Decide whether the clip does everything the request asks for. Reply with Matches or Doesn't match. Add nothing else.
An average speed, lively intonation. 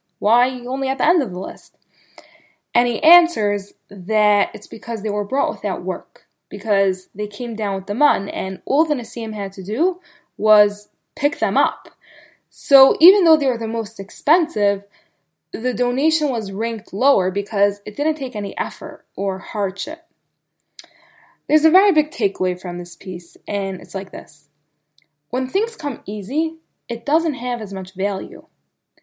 Matches